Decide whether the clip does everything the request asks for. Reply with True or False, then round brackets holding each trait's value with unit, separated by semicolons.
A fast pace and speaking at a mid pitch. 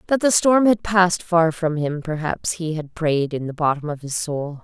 True (235 wpm; 165 Hz)